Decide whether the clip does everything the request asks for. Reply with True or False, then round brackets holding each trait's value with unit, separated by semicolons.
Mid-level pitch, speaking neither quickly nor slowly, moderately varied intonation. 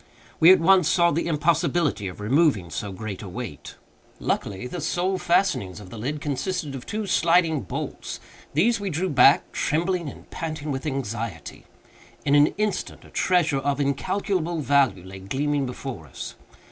False (145 Hz; 160 wpm; 6.5 semitones)